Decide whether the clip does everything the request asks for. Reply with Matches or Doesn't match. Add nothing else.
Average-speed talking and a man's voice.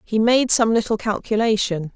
Doesn't match